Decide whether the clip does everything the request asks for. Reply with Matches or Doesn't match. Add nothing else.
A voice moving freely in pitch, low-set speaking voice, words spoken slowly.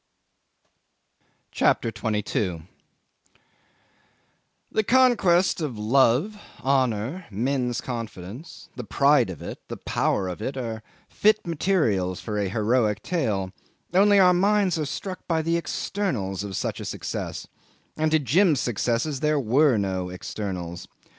Matches